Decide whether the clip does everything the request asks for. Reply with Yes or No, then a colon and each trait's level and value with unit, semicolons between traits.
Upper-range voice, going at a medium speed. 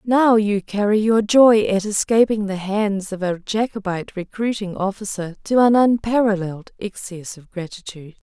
Yes: high, 205 Hz; average, 145 wpm